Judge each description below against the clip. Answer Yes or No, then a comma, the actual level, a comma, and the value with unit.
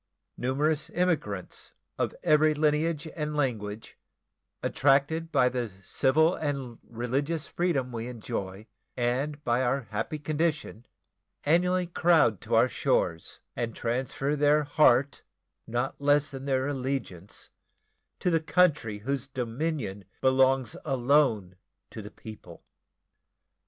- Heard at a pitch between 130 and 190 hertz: Yes, low, 135 Hz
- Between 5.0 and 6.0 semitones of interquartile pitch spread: No, average, 4.2 semitones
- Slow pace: Yes, slow, 115 wpm